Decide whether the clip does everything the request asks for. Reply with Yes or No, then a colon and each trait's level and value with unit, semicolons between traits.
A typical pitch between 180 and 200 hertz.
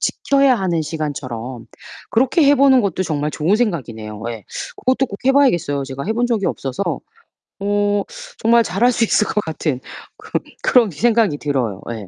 Yes: medium, 185 Hz